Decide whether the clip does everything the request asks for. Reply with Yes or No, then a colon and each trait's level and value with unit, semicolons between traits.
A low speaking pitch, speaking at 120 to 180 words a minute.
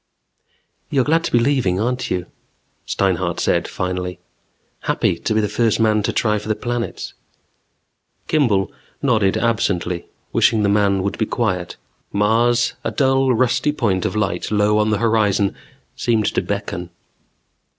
Yes: low, 105 Hz; average, 155 wpm